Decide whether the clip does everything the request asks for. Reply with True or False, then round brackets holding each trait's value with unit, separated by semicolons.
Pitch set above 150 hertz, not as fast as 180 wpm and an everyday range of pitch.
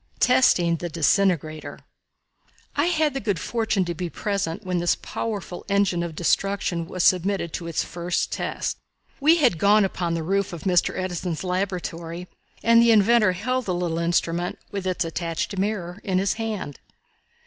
True (185 Hz; 160 wpm; 3.1 semitones)